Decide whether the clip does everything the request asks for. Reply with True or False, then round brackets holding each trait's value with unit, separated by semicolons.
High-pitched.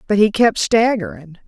True (210 Hz)